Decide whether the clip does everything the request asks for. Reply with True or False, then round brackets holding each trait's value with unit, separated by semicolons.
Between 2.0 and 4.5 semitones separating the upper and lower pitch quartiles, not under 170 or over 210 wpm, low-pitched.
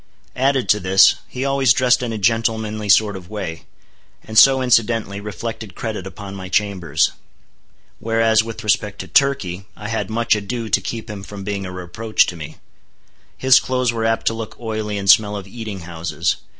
True (2.5 semitones; 180 wpm; 110 Hz)